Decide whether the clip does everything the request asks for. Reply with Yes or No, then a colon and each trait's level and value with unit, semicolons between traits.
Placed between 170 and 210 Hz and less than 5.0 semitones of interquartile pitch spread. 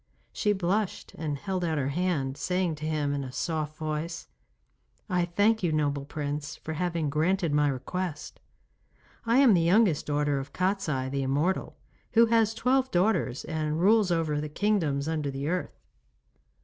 No: medium, 160 Hz; average, 4.2 semitones